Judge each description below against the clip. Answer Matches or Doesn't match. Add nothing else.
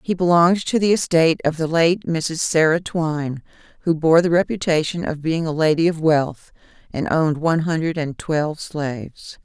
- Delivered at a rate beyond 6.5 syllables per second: Doesn't match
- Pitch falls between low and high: Matches